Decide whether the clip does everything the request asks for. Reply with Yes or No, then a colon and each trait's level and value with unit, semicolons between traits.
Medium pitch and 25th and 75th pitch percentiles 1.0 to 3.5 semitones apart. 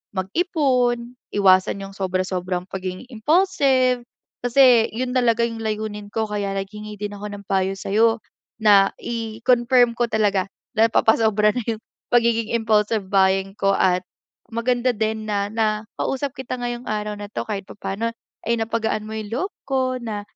No: high, 220 Hz; average, 2.9 semitones